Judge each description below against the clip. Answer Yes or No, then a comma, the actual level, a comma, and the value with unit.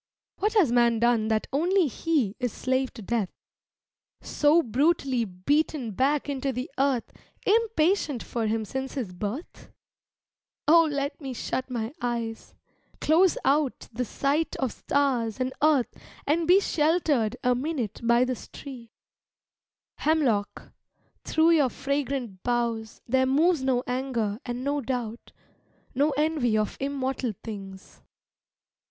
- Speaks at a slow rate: Yes, slow, 130 wpm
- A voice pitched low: No, very high, 260 Hz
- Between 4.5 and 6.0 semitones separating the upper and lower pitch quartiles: No, average, 4.1 semitones